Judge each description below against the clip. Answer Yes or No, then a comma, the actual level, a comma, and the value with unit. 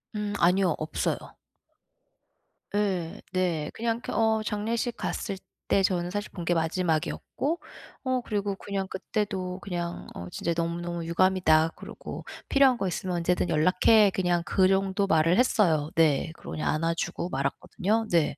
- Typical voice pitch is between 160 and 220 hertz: Yes, medium, 185 Hz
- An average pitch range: Yes, average, 3.5 semitones